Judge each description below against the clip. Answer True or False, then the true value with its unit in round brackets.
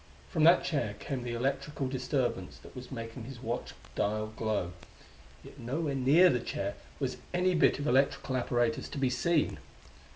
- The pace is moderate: True (165 wpm)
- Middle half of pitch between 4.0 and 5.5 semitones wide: False (3.5 semitones)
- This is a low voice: True (130 Hz)